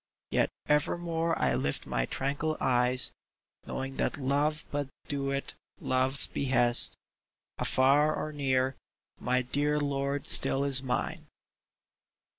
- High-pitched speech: No, medium, 140 Hz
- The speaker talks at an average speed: No, slow, 115 wpm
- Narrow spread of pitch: Yes, narrow, 2.2 semitones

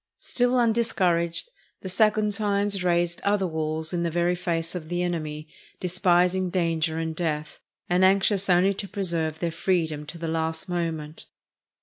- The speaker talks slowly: No, average, 145 wpm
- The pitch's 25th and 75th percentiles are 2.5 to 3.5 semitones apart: Yes, average, 2.8 semitones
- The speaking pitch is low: No, medium, 175 Hz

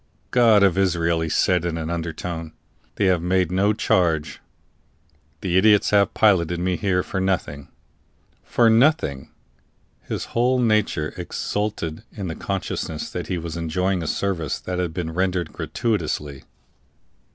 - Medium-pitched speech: No, very low, 90 Hz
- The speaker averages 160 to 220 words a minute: No, average, 140 wpm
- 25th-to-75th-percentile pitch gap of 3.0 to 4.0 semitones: Yes, average, 3.5 semitones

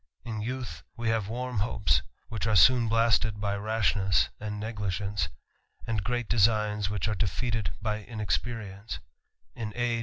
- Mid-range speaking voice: No, low, 105 Hz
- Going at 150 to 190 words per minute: Yes, average, 160 wpm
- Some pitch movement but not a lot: No, narrow, 2.1 semitones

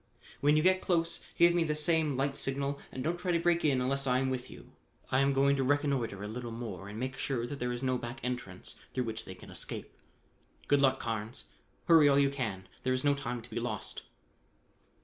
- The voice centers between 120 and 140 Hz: Yes, low, 135 Hz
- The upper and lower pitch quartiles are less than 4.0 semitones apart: Yes, average, 3.1 semitones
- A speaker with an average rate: No, fast, 225 wpm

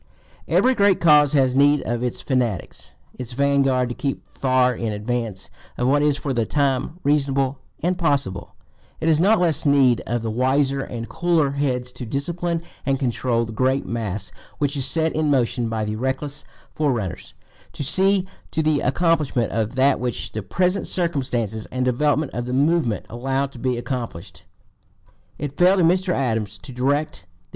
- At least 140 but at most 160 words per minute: No, average, 175 wpm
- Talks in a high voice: No, low, 135 Hz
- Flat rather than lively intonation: No, average, 3.7 semitones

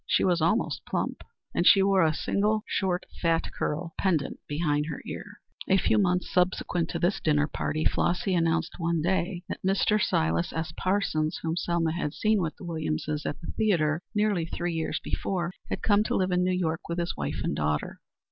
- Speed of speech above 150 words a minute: Yes, average, 195 wpm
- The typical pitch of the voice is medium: Yes, medium, 170 Hz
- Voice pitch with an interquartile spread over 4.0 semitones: No, average, 2.9 semitones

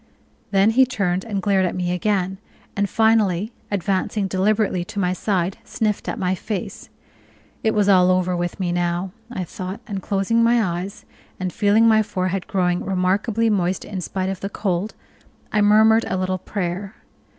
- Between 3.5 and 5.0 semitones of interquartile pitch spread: No, narrow, 2.4 semitones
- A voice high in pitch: Yes, high, 195 Hz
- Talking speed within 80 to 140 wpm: No, average, 170 wpm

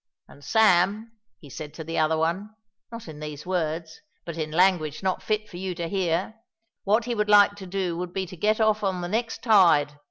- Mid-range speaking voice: Yes, medium, 180 Hz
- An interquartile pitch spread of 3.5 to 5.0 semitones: Yes, average, 4.5 semitones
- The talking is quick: Yes, fast, 215 wpm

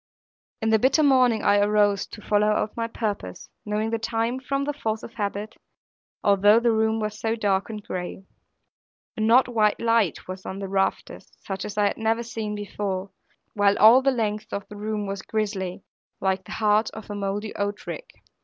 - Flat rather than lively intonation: Yes, narrow, 1.9 semitones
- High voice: Yes, high, 210 Hz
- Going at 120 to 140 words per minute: No, average, 190 wpm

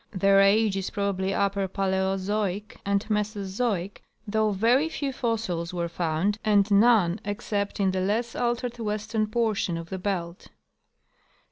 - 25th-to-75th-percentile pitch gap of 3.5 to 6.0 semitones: No, narrow, 2.4 semitones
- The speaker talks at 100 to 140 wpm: Yes, slow, 135 wpm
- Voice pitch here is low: No, high, 200 Hz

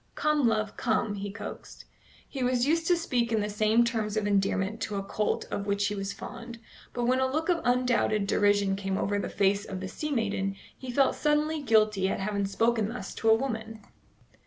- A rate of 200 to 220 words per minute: Yes, fast, 205 wpm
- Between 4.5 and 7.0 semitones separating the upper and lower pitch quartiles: No, average, 3.7 semitones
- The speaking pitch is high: Yes, high, 220 Hz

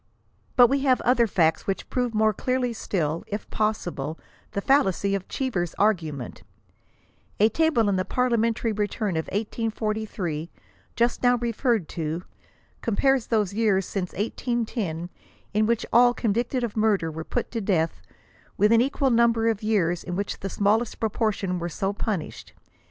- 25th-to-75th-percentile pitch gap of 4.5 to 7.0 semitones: No, average, 4.1 semitones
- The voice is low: No, high, 215 Hz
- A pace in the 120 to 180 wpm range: Yes, average, 155 wpm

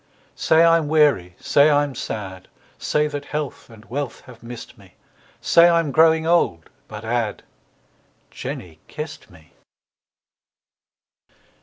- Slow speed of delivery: Yes, slow, 120 wpm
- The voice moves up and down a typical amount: No, wide, 6.4 semitones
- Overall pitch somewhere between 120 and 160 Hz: Yes, medium, 140 Hz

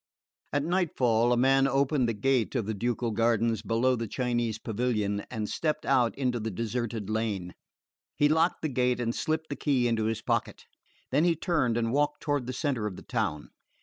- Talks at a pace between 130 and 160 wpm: No, average, 190 wpm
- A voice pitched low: Yes, low, 120 Hz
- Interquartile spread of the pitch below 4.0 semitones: Yes, average, 3.4 semitones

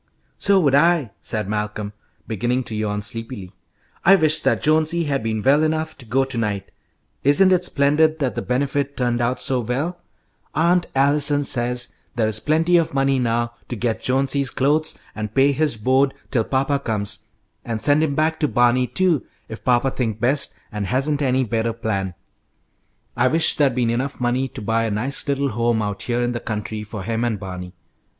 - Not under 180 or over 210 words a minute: Yes, average, 185 wpm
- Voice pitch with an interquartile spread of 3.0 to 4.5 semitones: Yes, average, 4.2 semitones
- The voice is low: Yes, low, 130 Hz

